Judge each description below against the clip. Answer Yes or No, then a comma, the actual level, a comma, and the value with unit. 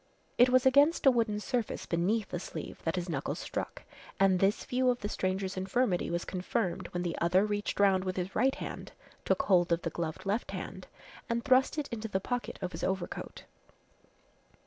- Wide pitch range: No, average, 4.9 semitones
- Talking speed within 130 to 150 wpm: No, average, 190 wpm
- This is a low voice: No, high, 195 Hz